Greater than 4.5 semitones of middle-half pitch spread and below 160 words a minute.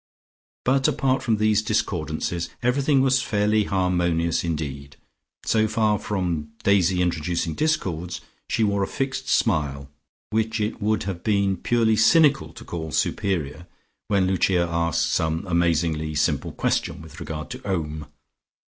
Yes: average, 5.0 semitones; slow, 135 wpm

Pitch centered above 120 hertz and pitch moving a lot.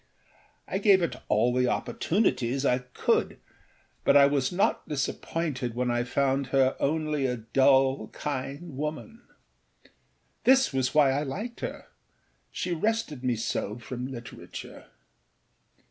No: low, 135 Hz; average, 3.8 semitones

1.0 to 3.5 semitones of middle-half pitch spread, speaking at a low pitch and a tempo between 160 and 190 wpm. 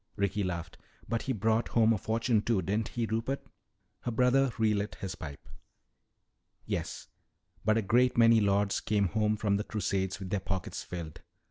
Yes: average, 2.8 semitones; low, 105 Hz; average, 165 wpm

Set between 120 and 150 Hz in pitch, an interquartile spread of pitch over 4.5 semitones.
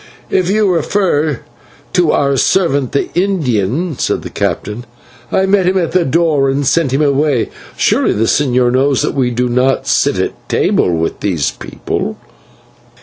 Yes: medium, 140 Hz; wide, 5.6 semitones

